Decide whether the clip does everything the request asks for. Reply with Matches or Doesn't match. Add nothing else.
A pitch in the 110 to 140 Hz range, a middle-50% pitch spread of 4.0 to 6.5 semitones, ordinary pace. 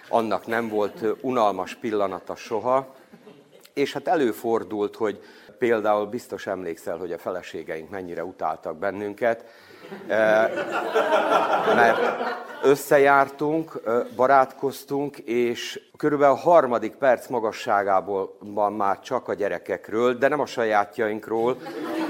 Doesn't match